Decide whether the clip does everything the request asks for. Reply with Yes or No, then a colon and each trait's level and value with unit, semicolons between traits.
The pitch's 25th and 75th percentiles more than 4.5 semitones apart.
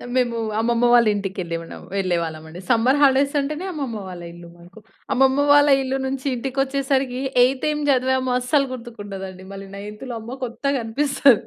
Yes: average, 5.2 semitones